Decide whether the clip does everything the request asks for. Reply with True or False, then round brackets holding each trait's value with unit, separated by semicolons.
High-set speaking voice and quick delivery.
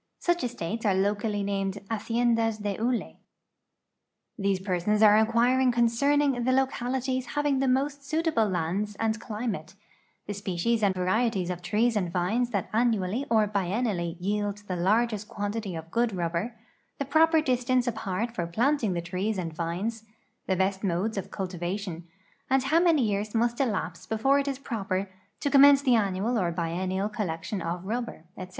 False (215 Hz; 160 wpm)